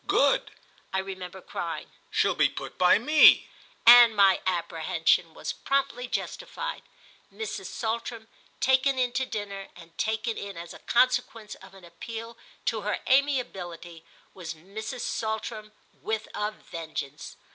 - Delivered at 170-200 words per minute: No, slow, 135 wpm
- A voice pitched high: Yes, high, 215 Hz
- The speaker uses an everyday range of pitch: Yes, average, 4.6 semitones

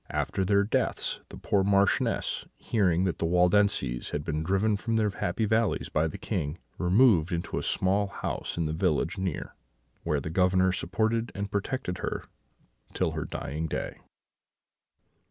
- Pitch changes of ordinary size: Yes, average, 3.7 semitones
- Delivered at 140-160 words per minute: Yes, average, 155 wpm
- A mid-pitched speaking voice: No, very low, 95 Hz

